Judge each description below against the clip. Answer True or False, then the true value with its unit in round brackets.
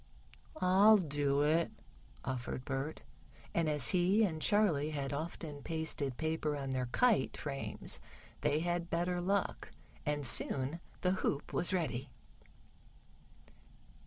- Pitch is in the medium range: True (155 Hz)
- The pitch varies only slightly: False (3.9 semitones)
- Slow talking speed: True (120 wpm)